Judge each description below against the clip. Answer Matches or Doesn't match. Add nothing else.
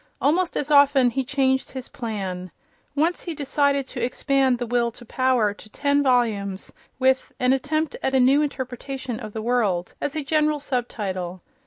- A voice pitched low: Doesn't match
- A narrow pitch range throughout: Doesn't match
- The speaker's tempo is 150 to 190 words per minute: Matches